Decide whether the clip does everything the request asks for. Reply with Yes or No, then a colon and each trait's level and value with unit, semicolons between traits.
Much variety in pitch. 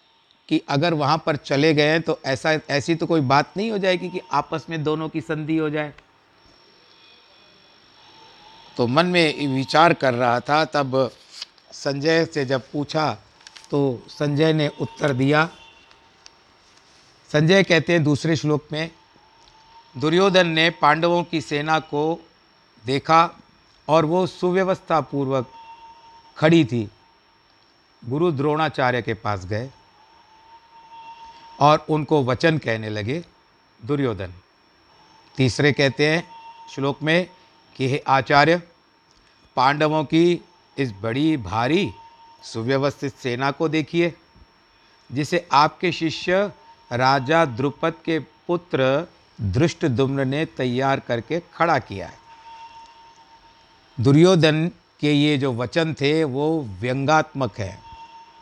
No: average, 4.1 semitones